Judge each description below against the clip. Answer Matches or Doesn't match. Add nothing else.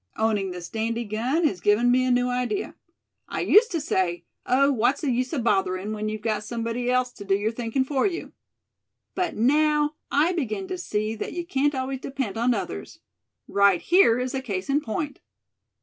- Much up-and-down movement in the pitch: Doesn't match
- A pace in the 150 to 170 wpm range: Doesn't match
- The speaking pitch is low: Doesn't match